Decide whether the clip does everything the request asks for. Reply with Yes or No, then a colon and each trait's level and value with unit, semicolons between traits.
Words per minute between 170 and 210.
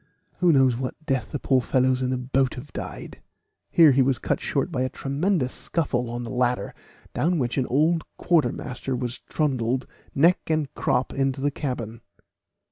Yes: average, 175 wpm